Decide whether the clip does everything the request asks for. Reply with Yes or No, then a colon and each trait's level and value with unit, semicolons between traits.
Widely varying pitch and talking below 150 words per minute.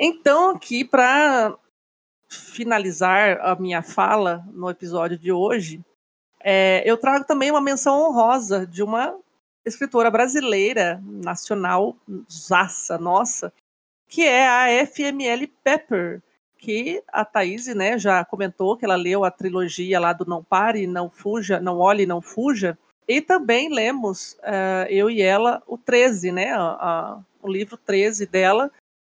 No: average, 4.9 semitones; average, 140 wpm